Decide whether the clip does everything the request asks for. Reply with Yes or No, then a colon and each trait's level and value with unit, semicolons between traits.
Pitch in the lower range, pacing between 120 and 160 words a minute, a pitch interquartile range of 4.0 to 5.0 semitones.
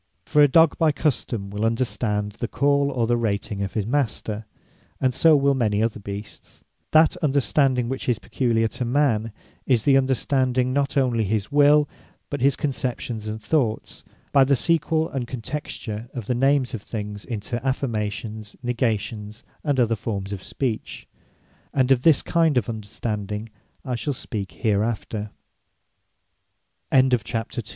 Yes: low, 120 Hz; average, 145 wpm; average, 4.3 semitones